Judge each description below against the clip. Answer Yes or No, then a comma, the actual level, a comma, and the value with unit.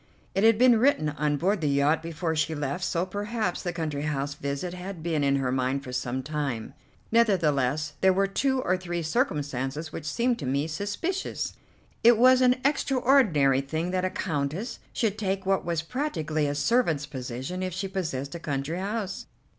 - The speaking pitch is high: No, medium, 165 Hz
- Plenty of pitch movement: Yes, wide, 5.8 semitones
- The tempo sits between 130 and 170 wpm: No, average, 180 wpm